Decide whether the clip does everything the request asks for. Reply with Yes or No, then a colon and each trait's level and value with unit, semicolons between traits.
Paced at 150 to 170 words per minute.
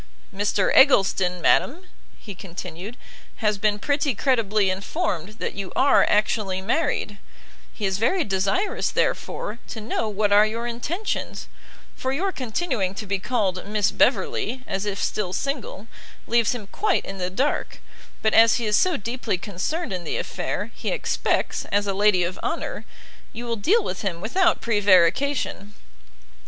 Yes: average, 155 wpm